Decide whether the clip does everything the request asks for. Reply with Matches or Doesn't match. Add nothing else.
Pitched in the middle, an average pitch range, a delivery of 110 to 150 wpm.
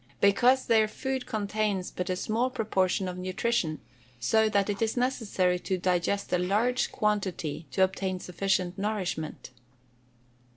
Doesn't match